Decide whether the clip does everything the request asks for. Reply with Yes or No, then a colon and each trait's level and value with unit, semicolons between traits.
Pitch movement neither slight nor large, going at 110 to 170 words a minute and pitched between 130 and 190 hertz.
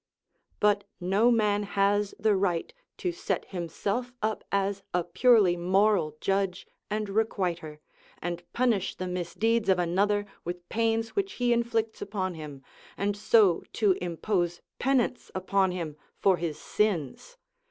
No: average, 3.7 semitones; slow, 135 wpm; high, 200 Hz